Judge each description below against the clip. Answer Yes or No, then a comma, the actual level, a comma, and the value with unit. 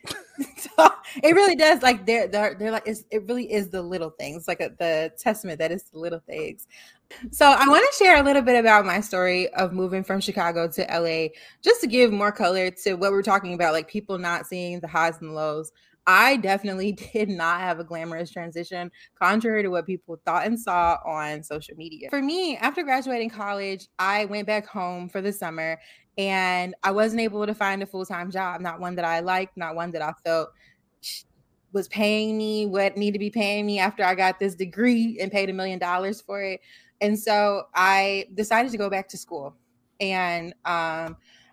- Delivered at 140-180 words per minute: No, average, 200 wpm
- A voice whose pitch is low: No, high, 195 Hz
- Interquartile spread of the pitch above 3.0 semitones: Yes, average, 3.8 semitones